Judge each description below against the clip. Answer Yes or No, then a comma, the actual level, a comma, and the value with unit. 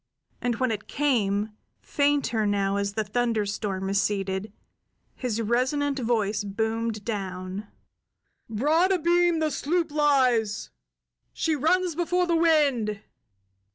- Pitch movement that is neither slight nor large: No, wide, 6.2 semitones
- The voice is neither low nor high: No, high, 230 Hz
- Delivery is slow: Yes, slow, 110 wpm